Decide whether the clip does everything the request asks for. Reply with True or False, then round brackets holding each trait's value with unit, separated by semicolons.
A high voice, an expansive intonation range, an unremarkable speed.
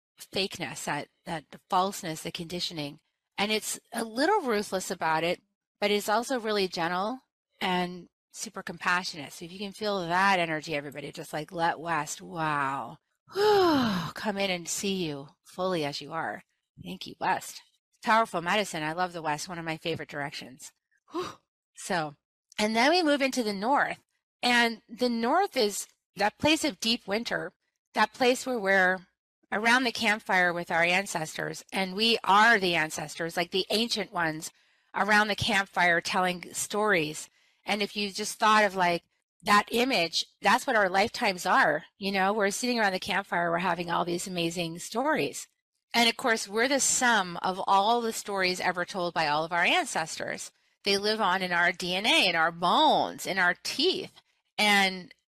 False (195 Hz; 4.6 semitones; 170 wpm)